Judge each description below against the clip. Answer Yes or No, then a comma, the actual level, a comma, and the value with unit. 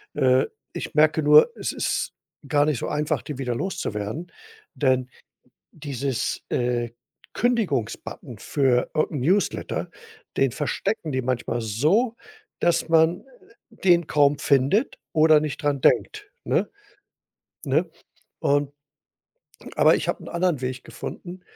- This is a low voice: No, medium, 145 Hz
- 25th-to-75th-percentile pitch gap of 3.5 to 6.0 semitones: Yes, average, 4.7 semitones